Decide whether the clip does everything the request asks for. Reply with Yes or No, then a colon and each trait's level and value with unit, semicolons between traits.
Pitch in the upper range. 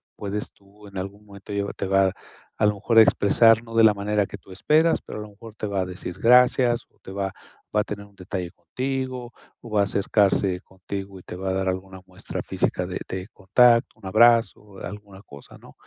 No: low, 100 Hz